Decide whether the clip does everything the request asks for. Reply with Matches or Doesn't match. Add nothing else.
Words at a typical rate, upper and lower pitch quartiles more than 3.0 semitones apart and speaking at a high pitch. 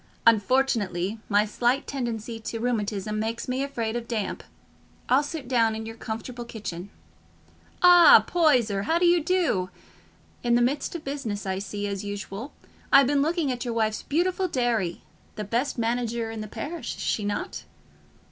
Matches